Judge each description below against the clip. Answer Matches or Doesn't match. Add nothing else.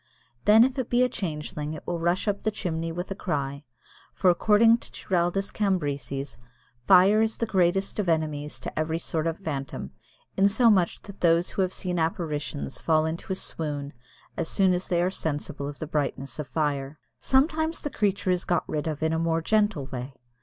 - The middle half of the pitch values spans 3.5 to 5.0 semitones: Matches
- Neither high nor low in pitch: Matches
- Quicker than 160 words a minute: Matches